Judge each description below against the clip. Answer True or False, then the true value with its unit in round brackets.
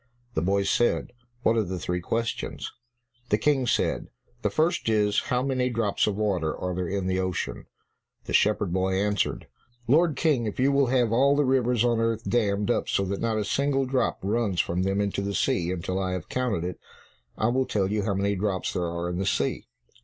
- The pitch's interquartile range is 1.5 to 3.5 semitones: False (4.6 semitones)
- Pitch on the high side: False (105 Hz)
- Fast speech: True (210 wpm)